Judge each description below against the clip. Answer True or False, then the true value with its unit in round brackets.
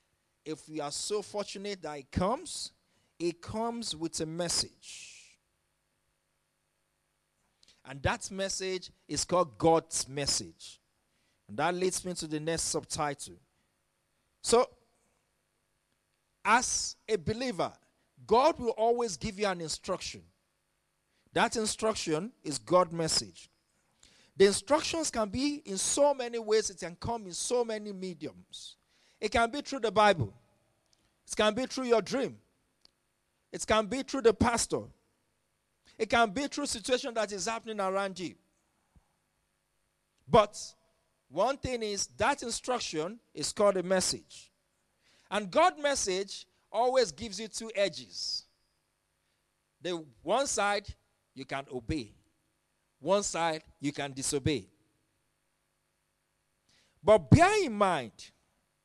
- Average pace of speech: False (120 wpm)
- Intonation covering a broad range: True (6.8 semitones)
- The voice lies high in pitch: True (195 Hz)